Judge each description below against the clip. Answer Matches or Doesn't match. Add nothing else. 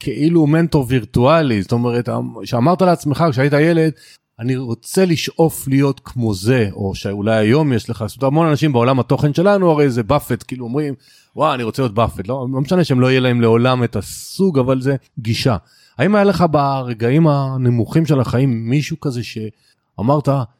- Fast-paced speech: Matches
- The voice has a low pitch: Matches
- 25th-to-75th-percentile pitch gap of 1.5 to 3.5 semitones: Doesn't match